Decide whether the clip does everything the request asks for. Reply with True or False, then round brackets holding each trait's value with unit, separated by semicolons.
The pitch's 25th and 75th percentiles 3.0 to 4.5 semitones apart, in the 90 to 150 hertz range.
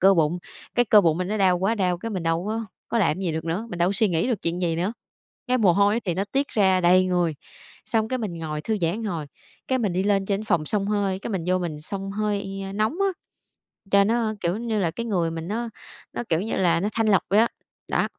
False (3.8 semitones; 195 Hz)